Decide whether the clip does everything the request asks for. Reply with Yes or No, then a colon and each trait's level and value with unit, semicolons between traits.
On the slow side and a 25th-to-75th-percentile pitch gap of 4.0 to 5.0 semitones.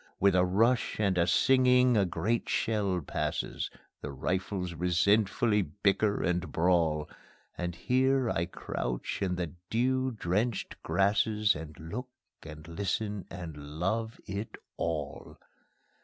Yes: slow, 125 wpm; average, 4.5 semitones